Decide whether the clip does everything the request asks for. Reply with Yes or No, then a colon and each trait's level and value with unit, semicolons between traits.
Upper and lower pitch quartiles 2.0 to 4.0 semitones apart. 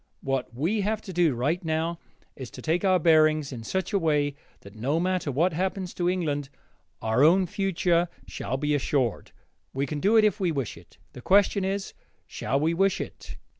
No: average, 4.7 semitones